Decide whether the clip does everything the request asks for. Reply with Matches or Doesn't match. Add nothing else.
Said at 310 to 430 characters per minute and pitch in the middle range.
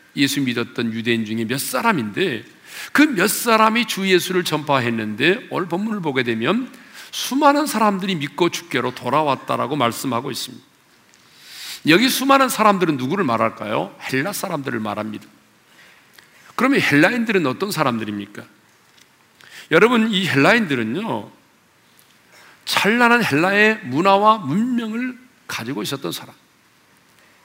Doesn't match